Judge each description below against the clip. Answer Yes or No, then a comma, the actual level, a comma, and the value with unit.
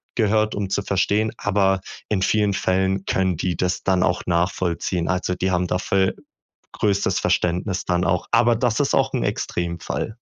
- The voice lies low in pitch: Yes, very low, 95 Hz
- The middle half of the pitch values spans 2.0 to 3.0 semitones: Yes, narrow, 2.3 semitones